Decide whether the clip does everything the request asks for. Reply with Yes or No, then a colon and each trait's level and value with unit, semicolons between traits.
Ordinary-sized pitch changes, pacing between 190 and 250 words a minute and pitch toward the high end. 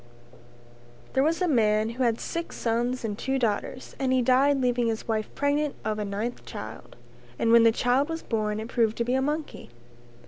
Yes: average, 3.2 semitones; fast, 205 wpm; high, 240 Hz